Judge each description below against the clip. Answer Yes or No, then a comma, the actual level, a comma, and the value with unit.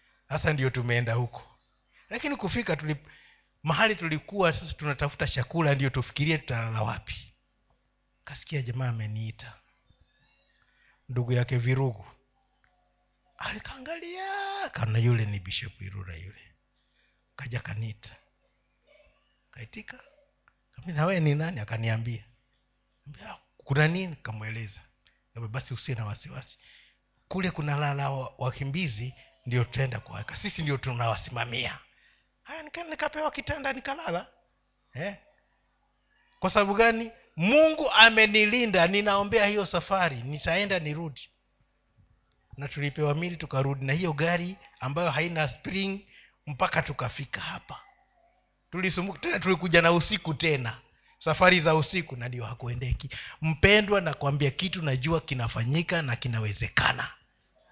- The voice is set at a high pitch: No, medium, 145 Hz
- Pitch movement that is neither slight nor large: No, wide, 7.1 semitones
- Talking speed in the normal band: No, slow, 95 wpm